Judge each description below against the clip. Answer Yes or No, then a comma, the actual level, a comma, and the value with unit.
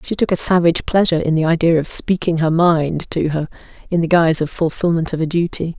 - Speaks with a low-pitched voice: No, medium, 165 Hz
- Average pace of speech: No, fast, 230 wpm